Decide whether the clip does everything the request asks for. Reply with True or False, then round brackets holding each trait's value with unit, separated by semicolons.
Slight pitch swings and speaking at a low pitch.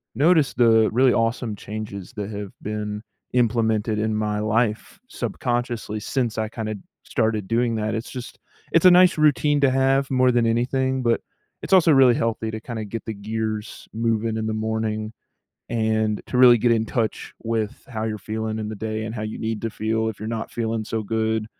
True (2.0 semitones; 110 Hz)